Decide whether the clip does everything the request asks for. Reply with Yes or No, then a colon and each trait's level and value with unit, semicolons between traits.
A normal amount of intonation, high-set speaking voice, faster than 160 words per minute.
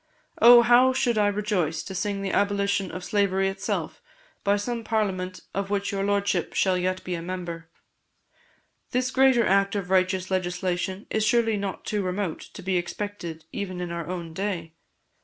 No: narrow, 2.2 semitones; high, 195 Hz; average, 170 wpm